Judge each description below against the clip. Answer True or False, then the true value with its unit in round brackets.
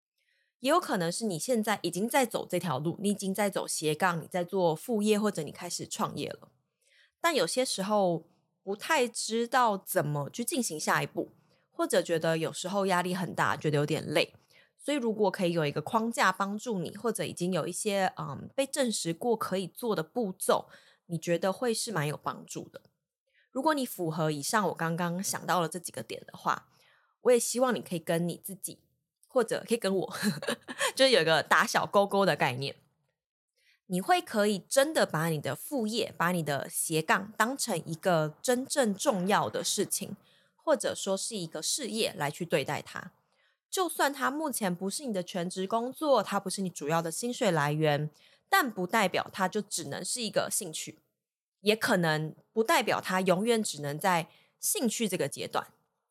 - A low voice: False (190 Hz)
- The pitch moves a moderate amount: False (5.7 semitones)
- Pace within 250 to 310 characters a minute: True (270 characters per minute)